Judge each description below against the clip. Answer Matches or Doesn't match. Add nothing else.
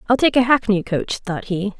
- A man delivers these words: Doesn't match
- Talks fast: Matches